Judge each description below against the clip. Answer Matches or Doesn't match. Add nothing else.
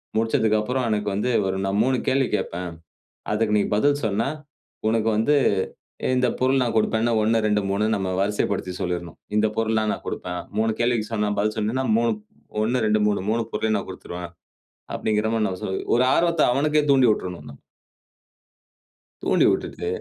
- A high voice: Doesn't match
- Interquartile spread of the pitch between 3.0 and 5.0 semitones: Doesn't match